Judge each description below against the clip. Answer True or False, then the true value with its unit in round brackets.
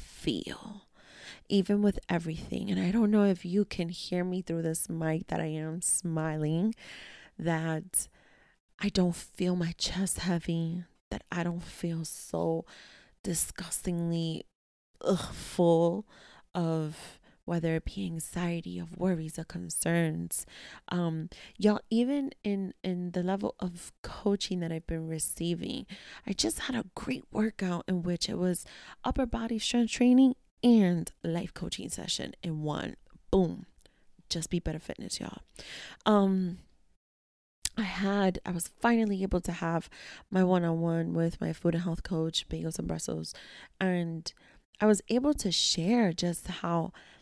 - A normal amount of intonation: True (3.2 semitones)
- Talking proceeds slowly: False (145 wpm)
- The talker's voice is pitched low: False (175 Hz)